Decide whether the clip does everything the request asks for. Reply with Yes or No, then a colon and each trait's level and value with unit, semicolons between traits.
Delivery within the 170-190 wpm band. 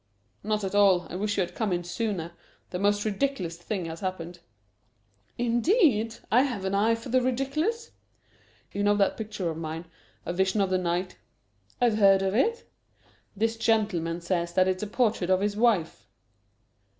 Yes: average, 175 wpm